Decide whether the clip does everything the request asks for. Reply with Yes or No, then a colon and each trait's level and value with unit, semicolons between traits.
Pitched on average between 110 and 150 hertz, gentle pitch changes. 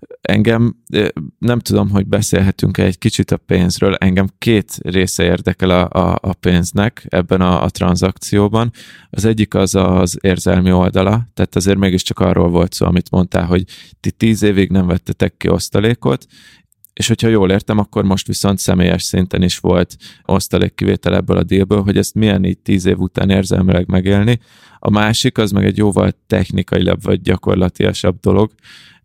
No: very low, 95 Hz; narrow, 2.3 semitones